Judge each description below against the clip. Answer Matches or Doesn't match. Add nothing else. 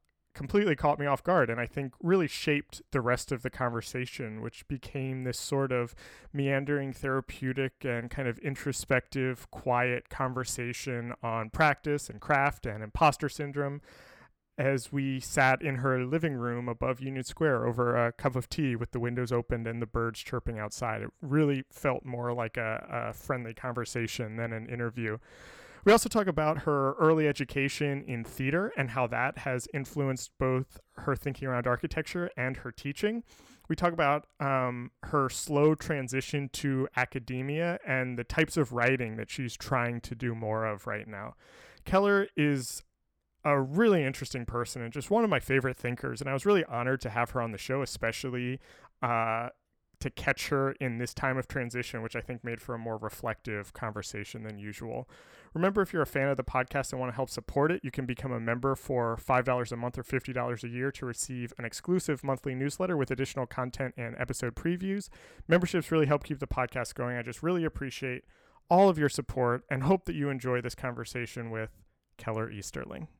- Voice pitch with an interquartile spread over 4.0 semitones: Doesn't match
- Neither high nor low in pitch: Doesn't match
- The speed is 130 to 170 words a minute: Doesn't match